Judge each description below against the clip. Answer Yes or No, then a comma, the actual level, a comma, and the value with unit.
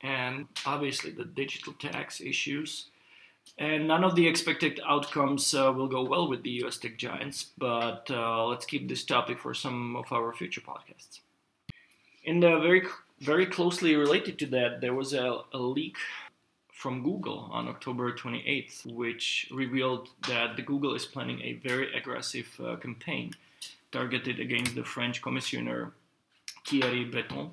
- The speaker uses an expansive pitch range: No, average, 3.8 semitones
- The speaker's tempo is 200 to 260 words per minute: No, average, 150 wpm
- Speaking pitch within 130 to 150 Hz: Yes, low, 135 Hz